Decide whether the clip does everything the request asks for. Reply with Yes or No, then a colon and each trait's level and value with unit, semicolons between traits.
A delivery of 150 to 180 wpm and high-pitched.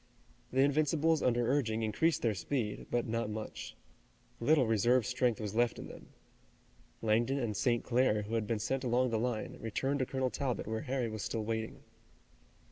No: average, 175 wpm; low, 120 Hz